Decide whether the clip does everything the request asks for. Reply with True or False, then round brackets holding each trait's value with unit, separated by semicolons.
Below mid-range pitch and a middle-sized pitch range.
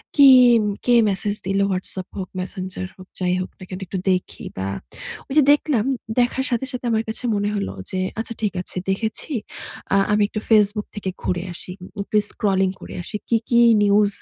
False (205 Hz; 3.1 semitones)